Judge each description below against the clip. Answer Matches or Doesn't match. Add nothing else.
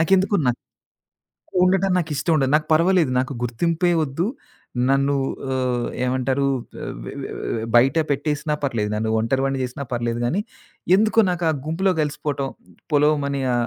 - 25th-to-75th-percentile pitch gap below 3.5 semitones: Doesn't match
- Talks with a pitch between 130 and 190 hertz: Matches